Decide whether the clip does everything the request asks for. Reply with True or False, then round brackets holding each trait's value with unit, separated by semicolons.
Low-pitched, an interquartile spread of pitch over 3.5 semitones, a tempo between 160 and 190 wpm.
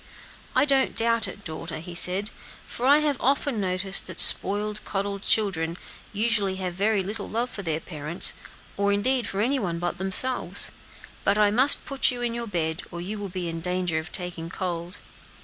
False (200 Hz; 4.5 semitones; 185 wpm)